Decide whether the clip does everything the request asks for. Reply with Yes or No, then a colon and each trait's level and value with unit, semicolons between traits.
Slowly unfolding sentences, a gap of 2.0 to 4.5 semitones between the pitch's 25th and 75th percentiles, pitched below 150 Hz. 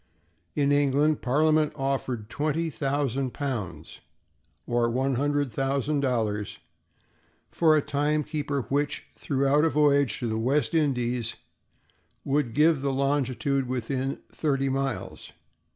Yes: slow, 120 wpm; narrow, 2.4 semitones; medium, 140 Hz